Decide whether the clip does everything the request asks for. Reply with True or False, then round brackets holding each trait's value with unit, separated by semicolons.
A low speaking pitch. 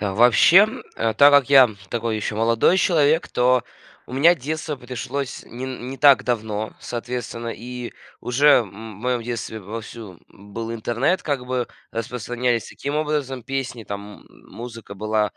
True (120 Hz)